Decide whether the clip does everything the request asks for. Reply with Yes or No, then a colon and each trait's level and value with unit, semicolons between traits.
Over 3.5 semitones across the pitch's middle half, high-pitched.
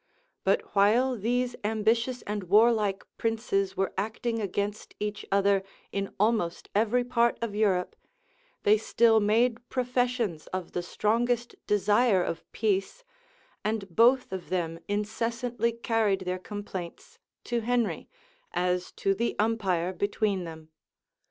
No: average, 3.2 semitones; high, 210 Hz